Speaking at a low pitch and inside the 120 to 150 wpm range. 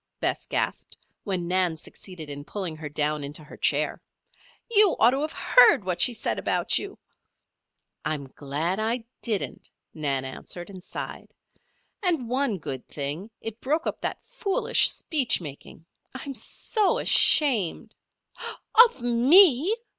No: high, 205 Hz; average, 145 wpm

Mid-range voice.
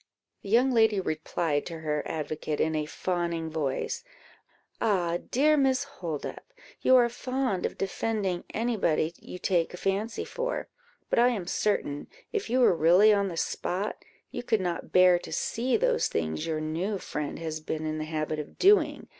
Yes: medium, 180 Hz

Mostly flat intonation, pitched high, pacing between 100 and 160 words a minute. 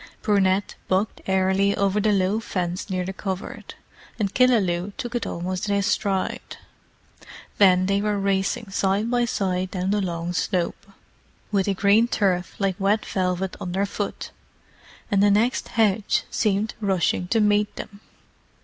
Yes: narrow, 1.9 semitones; high, 195 Hz; average, 150 wpm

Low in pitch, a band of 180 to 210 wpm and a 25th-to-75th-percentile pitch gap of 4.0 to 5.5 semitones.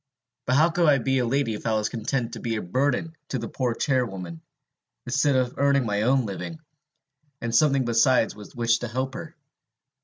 No: low, 125 Hz; average, 195 wpm; average, 3.2 semitones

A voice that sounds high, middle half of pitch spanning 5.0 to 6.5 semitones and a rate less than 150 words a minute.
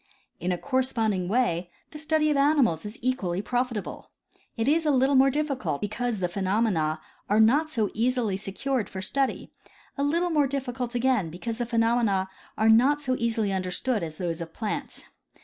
No: high, 235 Hz; wide, 5.5 semitones; average, 180 wpm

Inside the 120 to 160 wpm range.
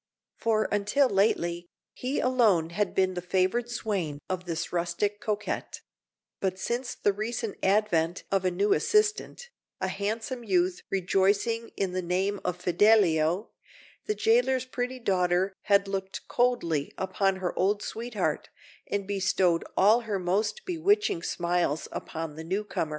Yes: average, 140 wpm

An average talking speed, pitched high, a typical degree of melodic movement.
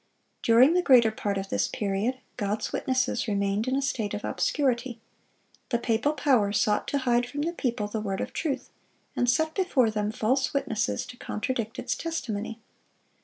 Yes: average, 170 wpm; high, 240 Hz; average, 3.9 semitones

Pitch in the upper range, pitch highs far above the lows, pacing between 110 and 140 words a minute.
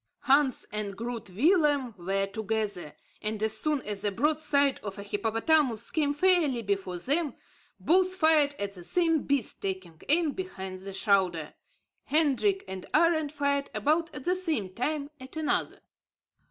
No: very high, 260 Hz; wide, 7.5 semitones; average, 155 wpm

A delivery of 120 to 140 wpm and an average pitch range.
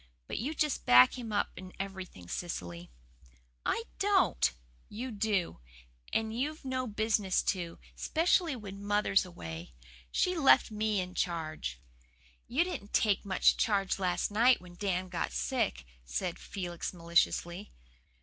Yes: slow, 135 wpm; average, 4.5 semitones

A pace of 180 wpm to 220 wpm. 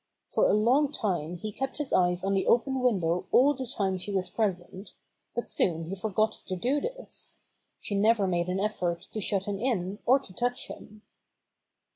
Yes: average, 190 wpm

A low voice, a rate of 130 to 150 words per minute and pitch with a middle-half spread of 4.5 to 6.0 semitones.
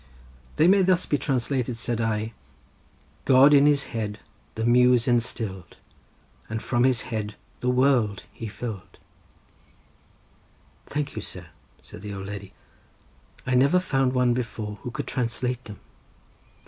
No: low, 120 Hz; average, 140 wpm; average, 3.1 semitones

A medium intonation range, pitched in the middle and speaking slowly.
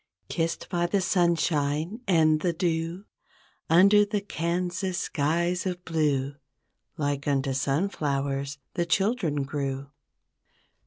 Yes: average, 3.9 semitones; medium, 165 Hz; slow, 105 wpm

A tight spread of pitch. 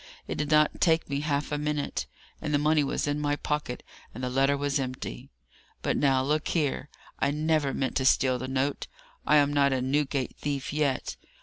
Yes: narrow, 1.9 semitones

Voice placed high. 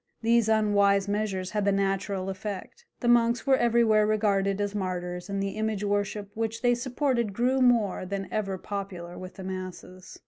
Yes: high, 205 Hz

